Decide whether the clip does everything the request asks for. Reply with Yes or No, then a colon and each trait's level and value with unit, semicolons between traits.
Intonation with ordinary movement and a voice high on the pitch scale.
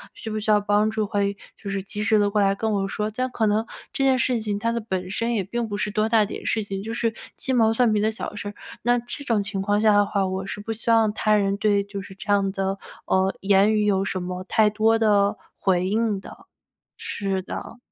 No: narrow, 2.0 semitones; high, 210 Hz